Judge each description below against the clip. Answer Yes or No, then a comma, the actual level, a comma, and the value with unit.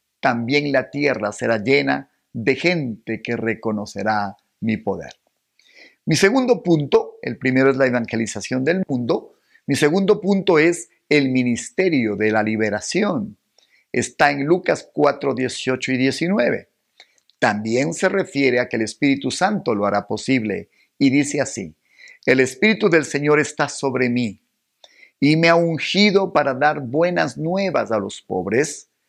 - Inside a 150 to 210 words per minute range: No, average, 140 wpm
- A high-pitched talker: No, low, 135 Hz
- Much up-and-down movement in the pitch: Yes, wide, 6.0 semitones